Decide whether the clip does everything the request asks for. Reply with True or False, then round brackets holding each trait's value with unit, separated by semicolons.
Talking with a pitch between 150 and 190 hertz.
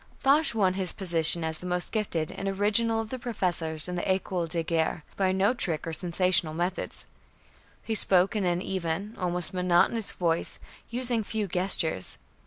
True (185 Hz)